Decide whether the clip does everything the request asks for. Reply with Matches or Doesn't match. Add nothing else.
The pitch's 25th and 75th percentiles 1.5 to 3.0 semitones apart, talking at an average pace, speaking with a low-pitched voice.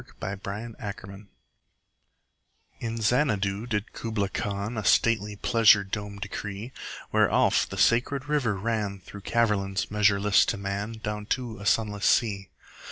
Doesn't match